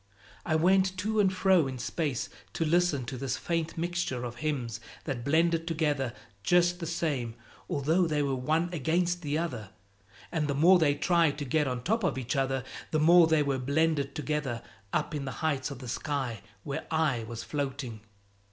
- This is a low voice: No, medium, 150 Hz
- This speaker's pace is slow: No, average, 185 wpm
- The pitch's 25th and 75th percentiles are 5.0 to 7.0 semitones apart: No, average, 4.1 semitones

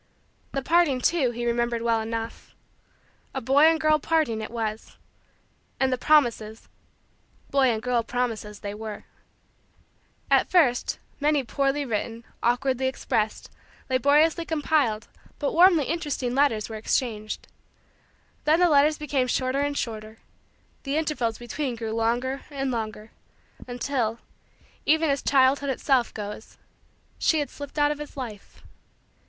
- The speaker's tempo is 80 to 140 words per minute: Yes, slow, 135 wpm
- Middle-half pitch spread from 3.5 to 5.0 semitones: Yes, average, 4.3 semitones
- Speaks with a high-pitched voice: Yes, very high, 260 Hz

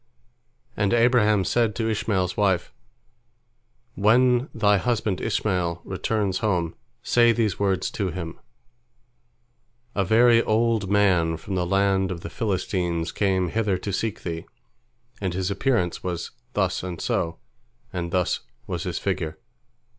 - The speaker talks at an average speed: No, slow, 130 wpm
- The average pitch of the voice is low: Yes, very low, 95 Hz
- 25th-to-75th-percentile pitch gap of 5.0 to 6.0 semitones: No, average, 3.4 semitones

